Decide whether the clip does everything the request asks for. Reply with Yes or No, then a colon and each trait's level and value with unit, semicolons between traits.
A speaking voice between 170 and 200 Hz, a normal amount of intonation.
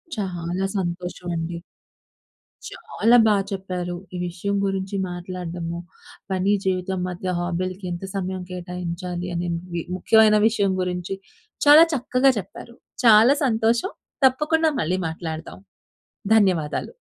Yes: medium, 185 Hz; average, 3.2 semitones